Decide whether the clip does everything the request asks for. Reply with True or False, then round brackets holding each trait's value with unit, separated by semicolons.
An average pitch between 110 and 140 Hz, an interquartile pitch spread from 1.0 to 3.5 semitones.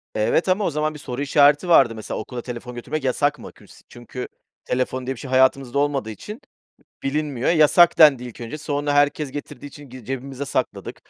True (135 Hz; 2.9 semitones)